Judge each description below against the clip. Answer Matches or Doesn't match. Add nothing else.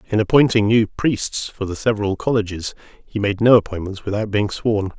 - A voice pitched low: Matches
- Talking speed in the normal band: Matches